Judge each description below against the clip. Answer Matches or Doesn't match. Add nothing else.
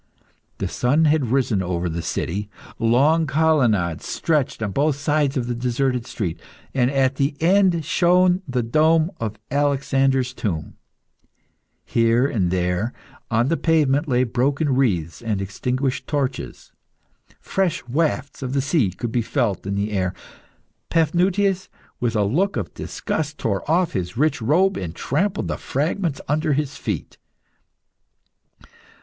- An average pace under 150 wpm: Matches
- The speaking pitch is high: Doesn't match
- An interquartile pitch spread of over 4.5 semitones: Matches